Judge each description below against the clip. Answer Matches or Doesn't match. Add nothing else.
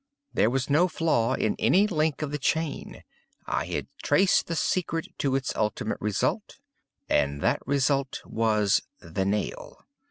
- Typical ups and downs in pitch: Doesn't match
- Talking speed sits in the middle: Matches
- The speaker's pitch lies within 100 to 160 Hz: Matches